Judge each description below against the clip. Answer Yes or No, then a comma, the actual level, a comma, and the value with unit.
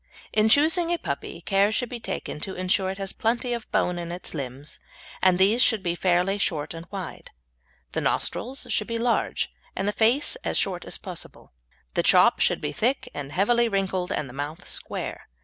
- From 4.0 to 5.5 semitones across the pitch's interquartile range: Yes, average, 4.9 semitones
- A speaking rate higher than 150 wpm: Yes, average, 195 wpm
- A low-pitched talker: No, high, 195 Hz